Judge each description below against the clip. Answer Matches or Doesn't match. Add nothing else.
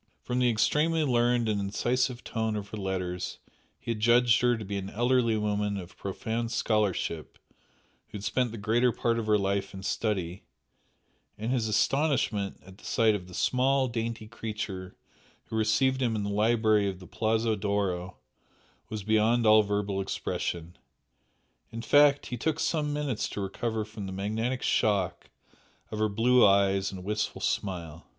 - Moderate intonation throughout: Matches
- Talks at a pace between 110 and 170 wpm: Matches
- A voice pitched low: Matches